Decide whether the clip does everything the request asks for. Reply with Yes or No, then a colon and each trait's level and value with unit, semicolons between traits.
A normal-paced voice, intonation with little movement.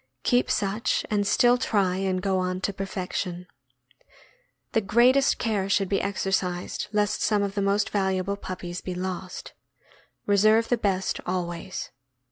Yes: average, 150 wpm; narrow, 2.0 semitones